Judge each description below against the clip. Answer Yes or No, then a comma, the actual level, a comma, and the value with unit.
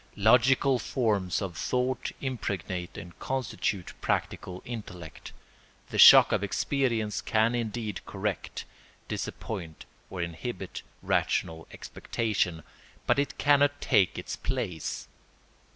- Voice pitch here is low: Yes, low, 110 Hz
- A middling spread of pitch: No, wide, 5.8 semitones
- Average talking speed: No, slow, 105 wpm